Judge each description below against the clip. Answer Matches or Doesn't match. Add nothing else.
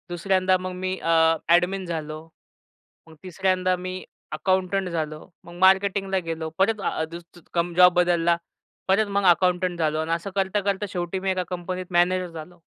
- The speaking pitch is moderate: Matches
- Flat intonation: Matches